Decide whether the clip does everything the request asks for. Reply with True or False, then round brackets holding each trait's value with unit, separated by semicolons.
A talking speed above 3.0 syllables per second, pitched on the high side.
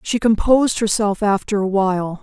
True (5.2 syllables/s; 205 Hz)